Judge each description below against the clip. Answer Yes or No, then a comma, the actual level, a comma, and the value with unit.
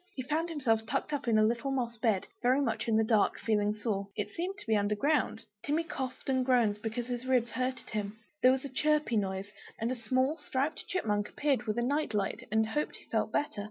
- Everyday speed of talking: No, fast, 230 wpm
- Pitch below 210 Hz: No, high, 240 Hz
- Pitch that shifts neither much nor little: Yes, average, 3.9 semitones